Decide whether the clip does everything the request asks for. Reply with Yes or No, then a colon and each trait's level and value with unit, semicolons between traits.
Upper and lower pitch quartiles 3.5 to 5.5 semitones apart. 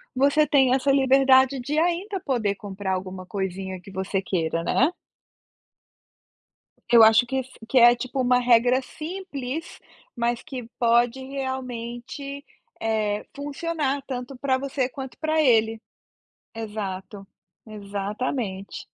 Yes: average, 4.5 semitones